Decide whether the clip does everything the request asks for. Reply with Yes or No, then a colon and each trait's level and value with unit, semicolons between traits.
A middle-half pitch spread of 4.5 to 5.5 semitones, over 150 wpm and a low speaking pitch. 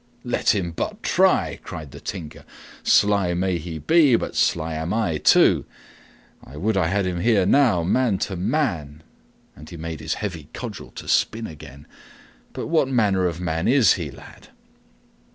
Yes: average, 5.1 semitones; average, 170 wpm; very low, 90 Hz